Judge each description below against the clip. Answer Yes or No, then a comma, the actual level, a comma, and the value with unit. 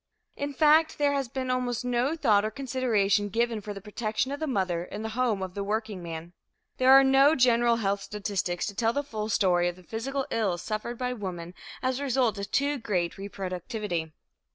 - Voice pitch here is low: No, high, 220 Hz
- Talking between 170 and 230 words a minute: Yes, average, 200 wpm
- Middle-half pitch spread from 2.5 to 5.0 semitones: Yes, average, 4.6 semitones